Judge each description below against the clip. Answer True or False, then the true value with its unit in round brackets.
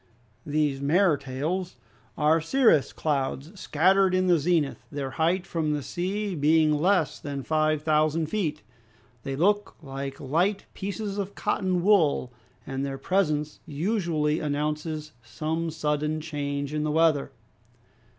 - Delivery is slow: True (130 wpm)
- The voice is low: False (155 Hz)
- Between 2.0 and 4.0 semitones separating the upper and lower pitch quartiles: True (3.6 semitones)